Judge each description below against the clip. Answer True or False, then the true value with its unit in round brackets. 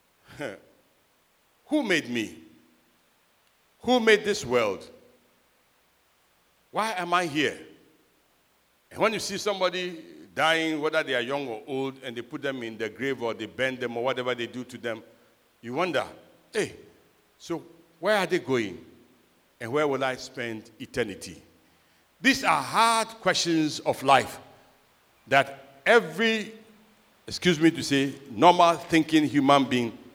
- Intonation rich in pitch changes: True (6.2 semitones)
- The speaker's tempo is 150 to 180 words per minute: False (140 wpm)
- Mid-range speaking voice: True (155 Hz)